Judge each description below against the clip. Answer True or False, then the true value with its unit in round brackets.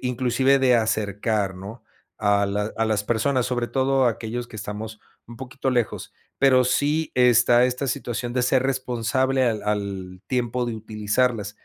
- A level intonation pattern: False (3.1 semitones)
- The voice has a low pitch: True (120 Hz)